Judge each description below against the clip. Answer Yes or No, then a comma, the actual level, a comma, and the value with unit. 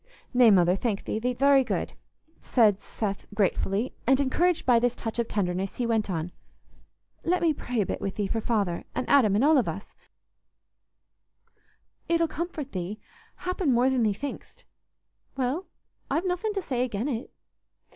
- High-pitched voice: Yes, high, 245 Hz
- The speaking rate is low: No, average, 165 wpm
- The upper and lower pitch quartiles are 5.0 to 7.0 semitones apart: Yes, wide, 5.4 semitones